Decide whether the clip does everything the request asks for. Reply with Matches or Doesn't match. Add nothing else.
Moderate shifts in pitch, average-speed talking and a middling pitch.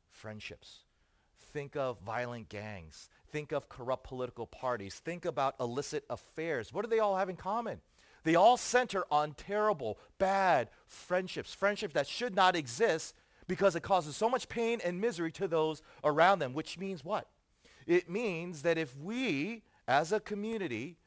Doesn't match